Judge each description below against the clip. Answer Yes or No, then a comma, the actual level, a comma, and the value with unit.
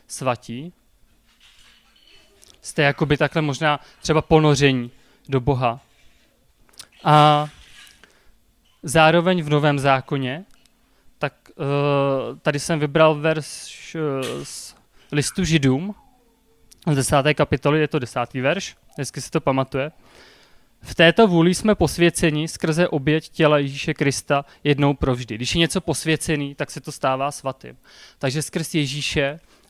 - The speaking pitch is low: No, medium, 150 Hz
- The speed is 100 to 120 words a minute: Yes, slow, 115 wpm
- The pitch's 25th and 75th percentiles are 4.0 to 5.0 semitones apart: No, narrow, 2.6 semitones